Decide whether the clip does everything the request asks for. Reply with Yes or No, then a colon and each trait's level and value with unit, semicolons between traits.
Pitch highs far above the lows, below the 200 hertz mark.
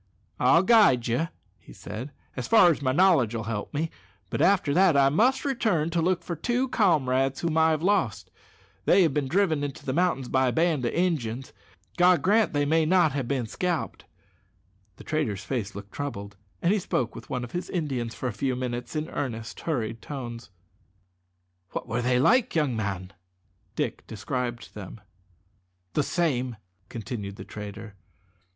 Yes: wide, 6.1 semitones; medium, 140 Hz